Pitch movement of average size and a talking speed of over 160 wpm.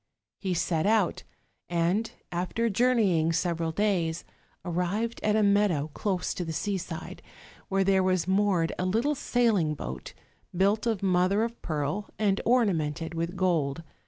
No: average, 4.0 semitones; average, 145 wpm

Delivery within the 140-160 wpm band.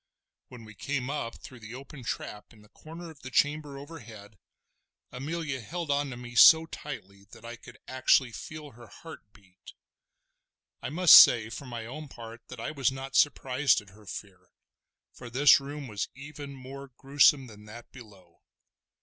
No: average, 175 wpm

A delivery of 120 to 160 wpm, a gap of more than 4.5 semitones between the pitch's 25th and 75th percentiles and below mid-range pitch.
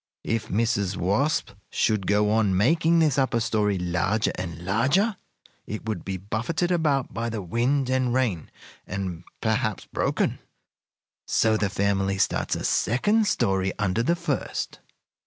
Yes: average, 140 wpm; average, 5.1 semitones; low, 110 Hz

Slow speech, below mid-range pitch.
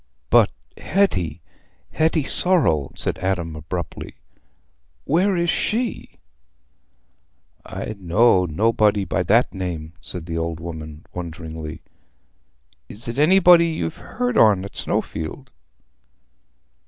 Yes: slow, 100 wpm; very low, 95 Hz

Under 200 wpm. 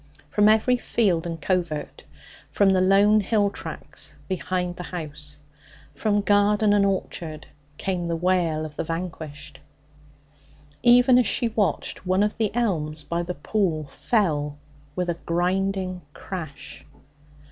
Yes: slow, 135 wpm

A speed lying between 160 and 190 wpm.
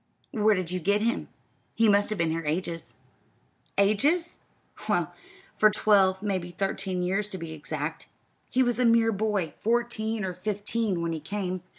Yes: average, 165 wpm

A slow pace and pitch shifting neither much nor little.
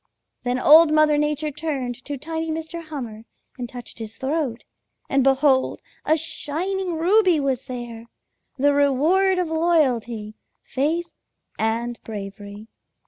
Yes: slow, 125 wpm; average, 5.0 semitones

